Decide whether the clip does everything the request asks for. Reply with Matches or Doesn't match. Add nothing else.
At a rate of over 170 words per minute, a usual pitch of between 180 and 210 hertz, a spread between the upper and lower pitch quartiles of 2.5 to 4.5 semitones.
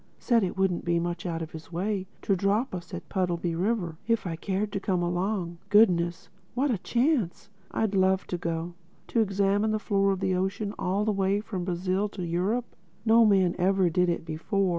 Matches